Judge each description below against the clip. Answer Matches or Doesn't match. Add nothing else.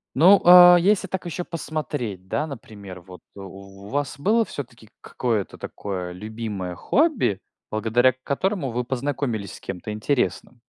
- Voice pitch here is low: Matches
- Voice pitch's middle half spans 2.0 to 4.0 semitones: Doesn't match